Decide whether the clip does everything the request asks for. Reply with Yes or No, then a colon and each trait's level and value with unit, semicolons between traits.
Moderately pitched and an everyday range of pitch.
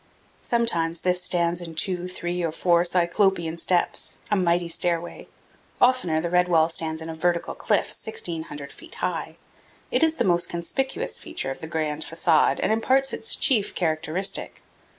No: medium, 175 Hz; narrow, 2.2 semitones